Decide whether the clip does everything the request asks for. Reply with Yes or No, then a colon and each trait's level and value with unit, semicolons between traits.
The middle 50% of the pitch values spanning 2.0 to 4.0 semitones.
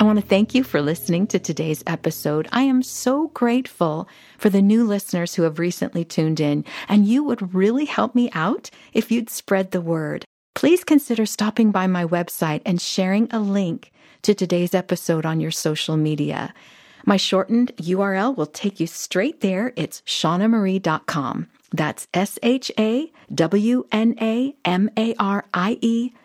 No: average, 5.1 semitones